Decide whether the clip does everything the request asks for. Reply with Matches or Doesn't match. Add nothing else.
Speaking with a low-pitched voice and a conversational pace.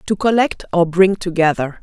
Doesn't match